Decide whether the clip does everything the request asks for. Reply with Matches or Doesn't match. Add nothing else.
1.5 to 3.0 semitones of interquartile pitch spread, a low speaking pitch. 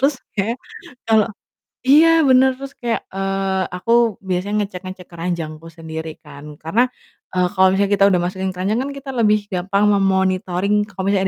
Doesn't match